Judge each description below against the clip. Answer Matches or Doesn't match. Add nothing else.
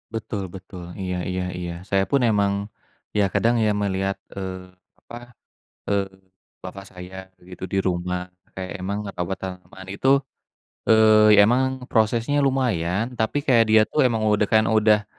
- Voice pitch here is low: Matches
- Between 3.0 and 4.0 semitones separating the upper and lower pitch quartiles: Matches